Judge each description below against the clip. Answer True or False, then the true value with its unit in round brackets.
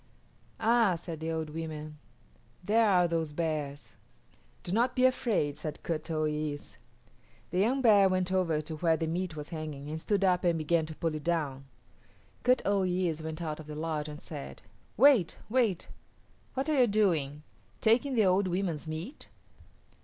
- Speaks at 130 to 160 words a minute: False (175 wpm)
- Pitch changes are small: False (4.4 semitones)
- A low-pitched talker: False (165 Hz)